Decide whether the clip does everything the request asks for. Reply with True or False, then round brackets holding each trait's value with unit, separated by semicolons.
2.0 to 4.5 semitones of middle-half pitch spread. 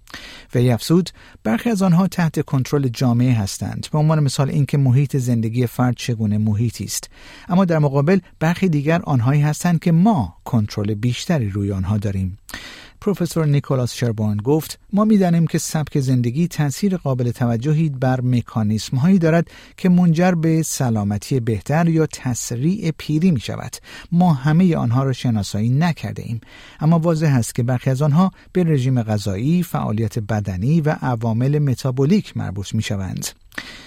False (5.6 semitones)